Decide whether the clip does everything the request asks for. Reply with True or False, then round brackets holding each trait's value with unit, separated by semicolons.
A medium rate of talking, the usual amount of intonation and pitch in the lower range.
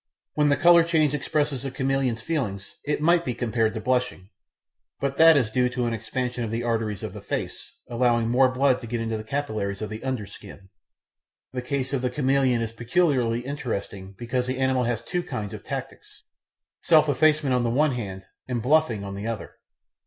True (195 wpm; 3.5 semitones; 125 Hz)